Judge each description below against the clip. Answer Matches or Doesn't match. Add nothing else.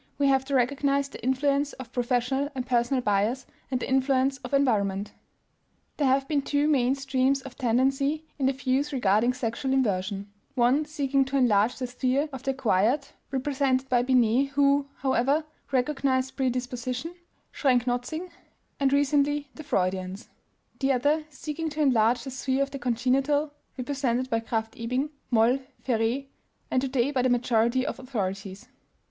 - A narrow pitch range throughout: Matches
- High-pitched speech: Matches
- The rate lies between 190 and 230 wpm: Doesn't match